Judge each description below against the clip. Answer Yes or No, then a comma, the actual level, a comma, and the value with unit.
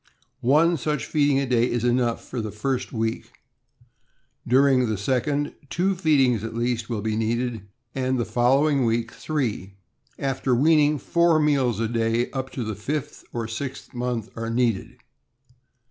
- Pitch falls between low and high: No, low, 125 Hz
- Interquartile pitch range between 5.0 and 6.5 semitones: No, average, 3.7 semitones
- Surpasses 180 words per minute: No, average, 155 wpm